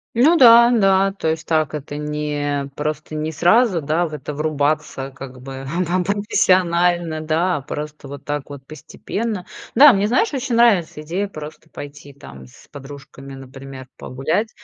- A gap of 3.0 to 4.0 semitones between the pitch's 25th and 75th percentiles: No, average, 4.8 semitones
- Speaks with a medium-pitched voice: Yes, medium, 155 Hz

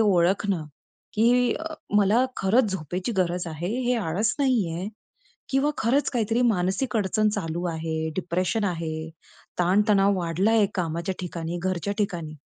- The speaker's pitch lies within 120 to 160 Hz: No, high, 190 Hz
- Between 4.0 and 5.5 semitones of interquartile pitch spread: Yes, average, 4.4 semitones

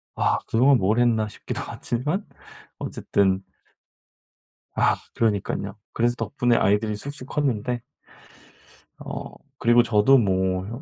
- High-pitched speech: No, low, 115 Hz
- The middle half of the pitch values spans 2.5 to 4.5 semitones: Yes, average, 3.2 semitones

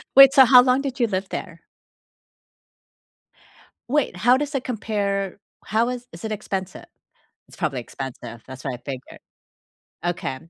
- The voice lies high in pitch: Yes, high, 210 Hz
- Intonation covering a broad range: Yes, wide, 7.0 semitones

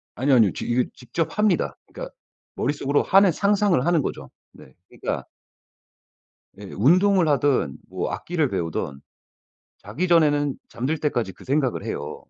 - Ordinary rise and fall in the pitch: No, wide, 6.0 semitones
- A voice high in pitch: No, medium, 145 Hz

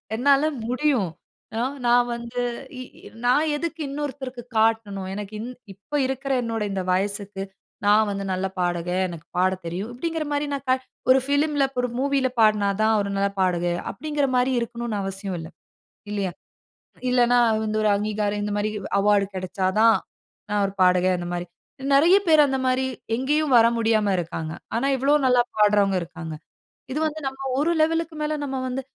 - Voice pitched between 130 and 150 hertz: No, high, 225 Hz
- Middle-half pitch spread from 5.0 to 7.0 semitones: Yes, wide, 5.5 semitones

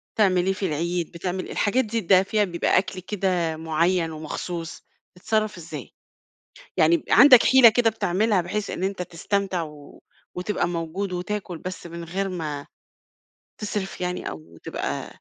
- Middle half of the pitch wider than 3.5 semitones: No, average, 3.2 semitones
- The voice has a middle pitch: Yes, medium, 180 Hz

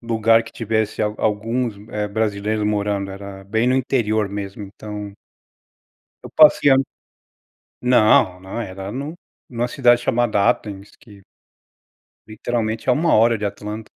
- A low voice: Yes, low, 110 Hz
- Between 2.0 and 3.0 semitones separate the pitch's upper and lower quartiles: Yes, average, 2.7 semitones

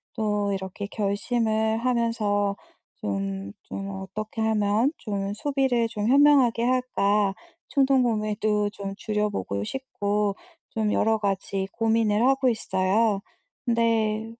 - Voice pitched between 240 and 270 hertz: No, high, 215 Hz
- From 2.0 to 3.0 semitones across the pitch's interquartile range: Yes, narrow, 2.4 semitones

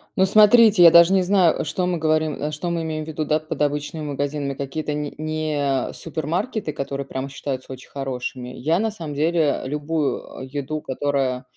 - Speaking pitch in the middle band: Yes, medium, 150 Hz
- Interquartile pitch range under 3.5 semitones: Yes, average, 2.9 semitones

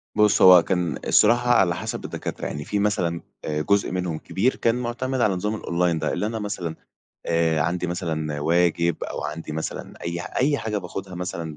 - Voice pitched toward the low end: Yes, very low, 90 Hz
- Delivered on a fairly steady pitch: No, average, 3.9 semitones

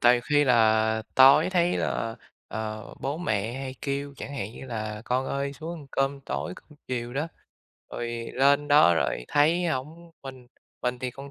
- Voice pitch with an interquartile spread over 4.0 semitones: No, average, 3.6 semitones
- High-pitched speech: No, low, 135 Hz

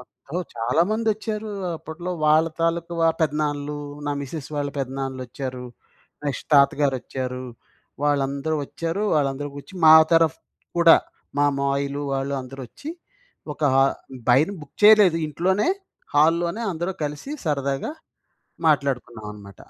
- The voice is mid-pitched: Yes, medium, 145 Hz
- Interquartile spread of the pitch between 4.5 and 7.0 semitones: No, average, 3.5 semitones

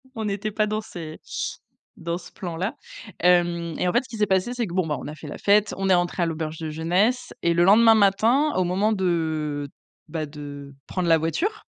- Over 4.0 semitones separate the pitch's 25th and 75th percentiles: Yes, average, 4.4 semitones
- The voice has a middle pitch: Yes, medium, 180 Hz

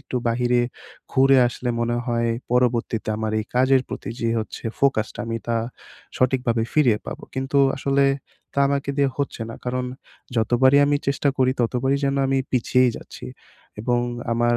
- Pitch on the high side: No, low, 125 Hz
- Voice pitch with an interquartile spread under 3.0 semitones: Yes, narrow, 2.5 semitones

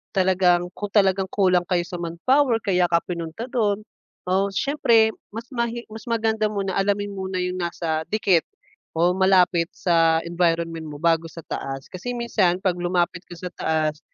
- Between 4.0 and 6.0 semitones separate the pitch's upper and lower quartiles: No, average, 3.3 semitones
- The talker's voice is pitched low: No, medium, 185 Hz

